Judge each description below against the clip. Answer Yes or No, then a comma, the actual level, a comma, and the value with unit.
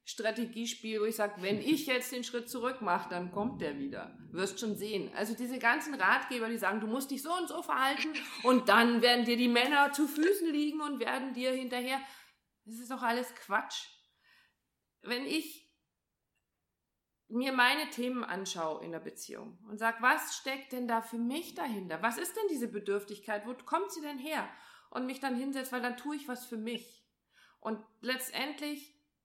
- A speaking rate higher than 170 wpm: Yes, average, 185 wpm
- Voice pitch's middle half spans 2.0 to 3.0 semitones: No, average, 3.5 semitones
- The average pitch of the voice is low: No, high, 245 Hz